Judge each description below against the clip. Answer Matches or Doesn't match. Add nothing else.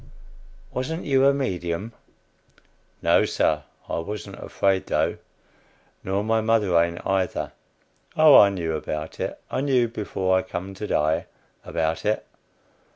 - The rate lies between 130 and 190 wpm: Matches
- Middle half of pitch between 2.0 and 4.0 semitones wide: Doesn't match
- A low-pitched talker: Matches